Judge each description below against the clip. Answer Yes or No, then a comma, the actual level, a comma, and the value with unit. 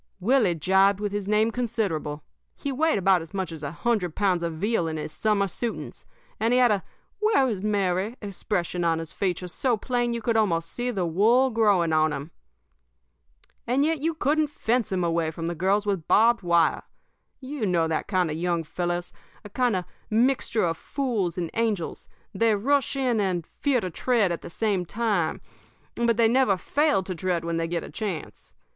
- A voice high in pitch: Yes, high, 200 Hz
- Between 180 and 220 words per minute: Yes, average, 200 wpm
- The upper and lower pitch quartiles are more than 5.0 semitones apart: Yes, wide, 5.4 semitones